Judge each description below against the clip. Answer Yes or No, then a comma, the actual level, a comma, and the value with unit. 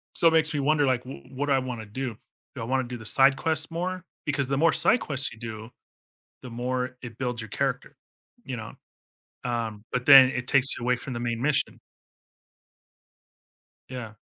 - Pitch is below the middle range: Yes, low, 130 Hz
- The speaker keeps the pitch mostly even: No, average, 3.1 semitones